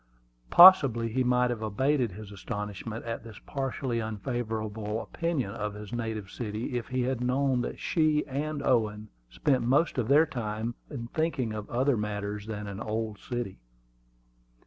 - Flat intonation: No, average, 3.7 semitones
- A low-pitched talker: Yes, low, 115 Hz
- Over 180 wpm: No, average, 155 wpm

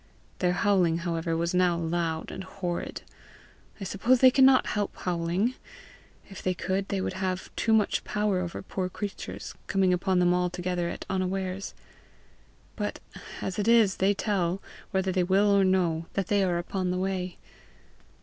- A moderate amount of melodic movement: No, narrow, 1.9 semitones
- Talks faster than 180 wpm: No, average, 160 wpm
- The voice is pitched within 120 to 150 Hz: No, medium, 185 Hz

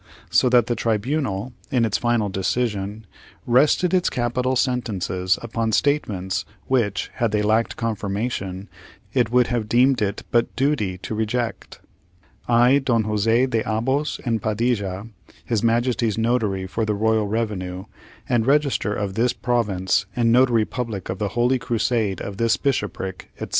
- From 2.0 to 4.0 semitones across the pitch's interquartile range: Yes, average, 3.2 semitones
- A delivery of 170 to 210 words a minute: No, average, 150 wpm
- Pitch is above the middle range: No, low, 115 Hz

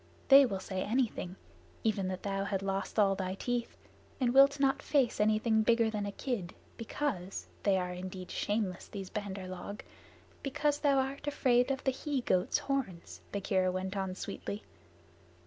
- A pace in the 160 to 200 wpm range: Yes, average, 165 wpm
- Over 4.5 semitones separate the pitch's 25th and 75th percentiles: Yes, average, 5.3 semitones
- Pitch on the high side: Yes, high, 210 Hz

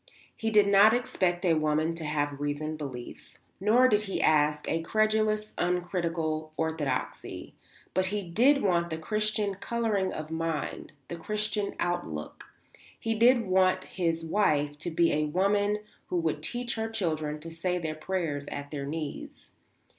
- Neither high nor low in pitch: Yes, medium, 175 Hz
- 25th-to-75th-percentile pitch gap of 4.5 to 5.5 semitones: Yes, average, 5.0 semitones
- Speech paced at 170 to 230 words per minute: No, average, 155 wpm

